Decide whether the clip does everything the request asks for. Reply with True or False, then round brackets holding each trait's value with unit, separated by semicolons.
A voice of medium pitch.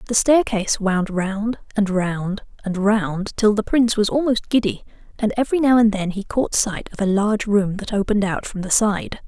False (210 Hz)